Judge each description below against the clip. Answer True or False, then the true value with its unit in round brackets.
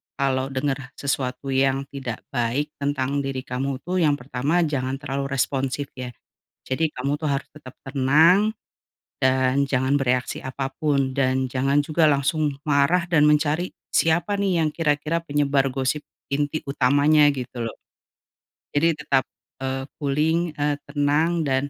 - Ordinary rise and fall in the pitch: False (2.3 semitones)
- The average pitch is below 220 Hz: True (140 Hz)